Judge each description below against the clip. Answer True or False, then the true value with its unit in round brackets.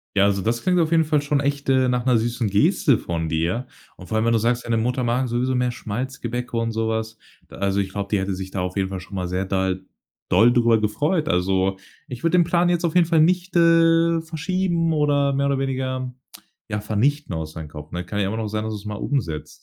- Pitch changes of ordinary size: False (6.4 semitones)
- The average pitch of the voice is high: False (120 Hz)